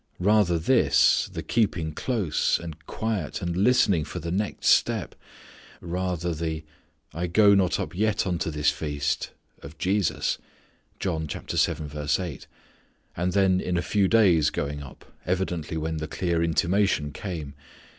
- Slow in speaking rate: Yes, slow, 130 wpm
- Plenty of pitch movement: No, average, 3.6 semitones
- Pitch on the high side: No, very low, 85 Hz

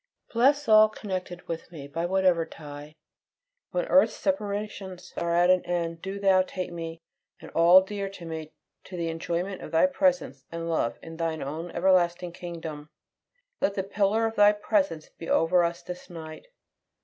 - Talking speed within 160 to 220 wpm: Yes, average, 170 wpm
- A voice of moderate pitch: Yes, medium, 175 Hz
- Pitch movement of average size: Yes, average, 3.1 semitones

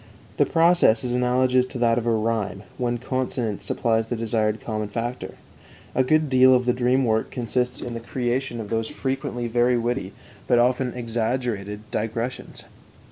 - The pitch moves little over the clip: Yes, narrow, 2.1 semitones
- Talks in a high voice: No, low, 120 Hz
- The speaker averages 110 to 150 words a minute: No, average, 160 wpm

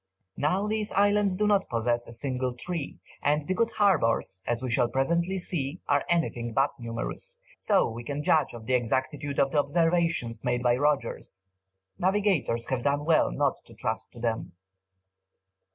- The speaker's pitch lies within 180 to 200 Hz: No, medium, 140 Hz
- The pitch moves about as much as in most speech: No, wide, 6.5 semitones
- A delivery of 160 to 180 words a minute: Yes, average, 170 wpm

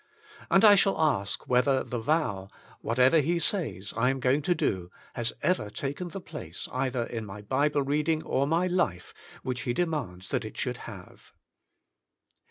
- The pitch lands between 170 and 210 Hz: No, low, 135 Hz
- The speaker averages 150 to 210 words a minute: Yes, average, 170 wpm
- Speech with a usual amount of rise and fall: No, wide, 5.9 semitones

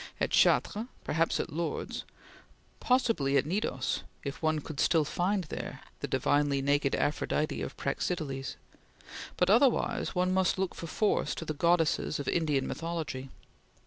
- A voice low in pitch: No, medium, 160 Hz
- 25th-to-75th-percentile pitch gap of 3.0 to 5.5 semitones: Yes, average, 4.0 semitones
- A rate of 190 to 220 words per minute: No, average, 145 wpm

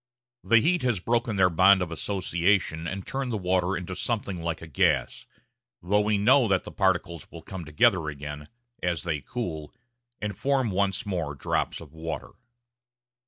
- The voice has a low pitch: Yes, very low, 90 Hz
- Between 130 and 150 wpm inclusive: No, average, 165 wpm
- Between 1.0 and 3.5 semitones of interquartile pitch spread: No, average, 4.0 semitones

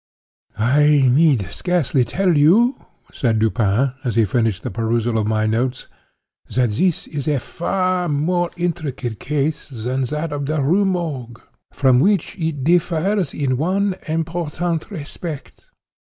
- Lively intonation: Yes, wide, 5.8 semitones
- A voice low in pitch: No, medium, 145 Hz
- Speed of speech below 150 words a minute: Yes, average, 140 wpm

